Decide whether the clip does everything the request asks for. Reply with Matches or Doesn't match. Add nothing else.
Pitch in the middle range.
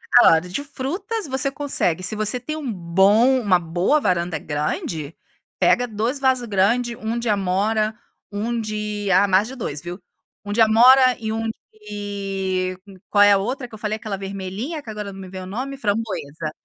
Doesn't match